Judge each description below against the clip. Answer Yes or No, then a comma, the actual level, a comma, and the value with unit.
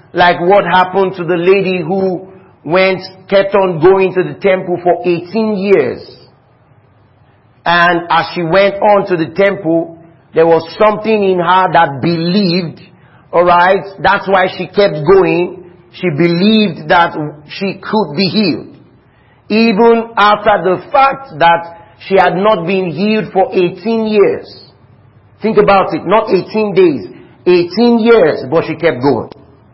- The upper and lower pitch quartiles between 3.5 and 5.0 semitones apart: No, average, 2.9 semitones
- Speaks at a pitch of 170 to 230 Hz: Yes, medium, 185 Hz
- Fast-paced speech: No, average, 140 wpm